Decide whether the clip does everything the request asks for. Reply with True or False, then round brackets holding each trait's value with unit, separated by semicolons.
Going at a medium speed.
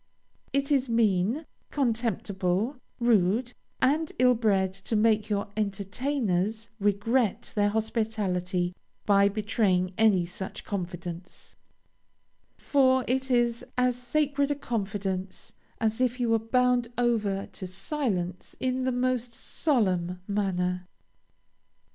False (110 wpm)